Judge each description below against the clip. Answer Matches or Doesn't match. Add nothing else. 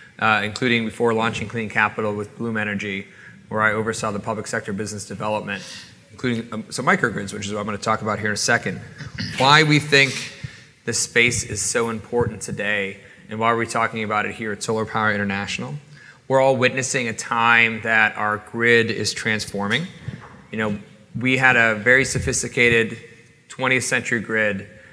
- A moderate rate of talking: Matches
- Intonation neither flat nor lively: Doesn't match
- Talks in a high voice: Doesn't match